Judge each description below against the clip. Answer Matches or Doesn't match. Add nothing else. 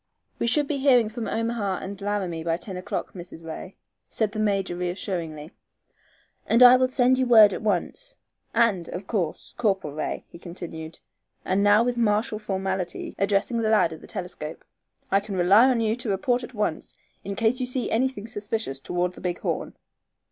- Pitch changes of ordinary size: Matches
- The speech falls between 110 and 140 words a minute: Doesn't match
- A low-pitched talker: Doesn't match